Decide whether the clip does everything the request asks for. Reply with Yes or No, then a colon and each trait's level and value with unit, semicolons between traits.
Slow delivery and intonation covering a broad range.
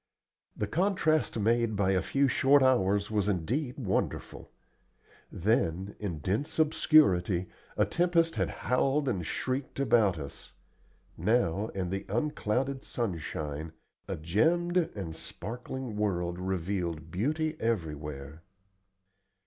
Yes: slow, 110 wpm; wide, 7.3 semitones